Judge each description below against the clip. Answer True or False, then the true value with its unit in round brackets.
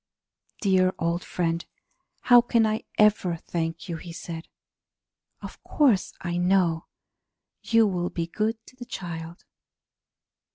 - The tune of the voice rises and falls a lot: False (4.2 semitones)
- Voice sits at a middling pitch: True (180 Hz)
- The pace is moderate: False (125 wpm)